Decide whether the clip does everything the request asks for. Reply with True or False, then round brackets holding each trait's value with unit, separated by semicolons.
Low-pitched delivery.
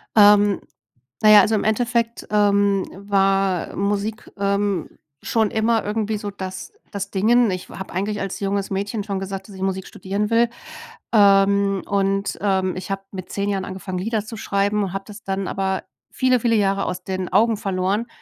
False (200 Hz)